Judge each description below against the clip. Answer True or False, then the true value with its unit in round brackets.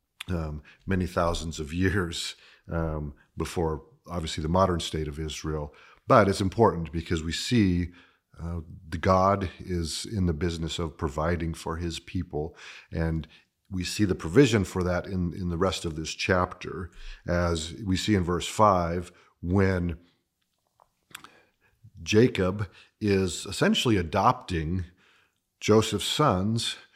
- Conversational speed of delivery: False (130 wpm)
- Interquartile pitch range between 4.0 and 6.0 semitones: False (2.6 semitones)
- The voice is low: True (90 Hz)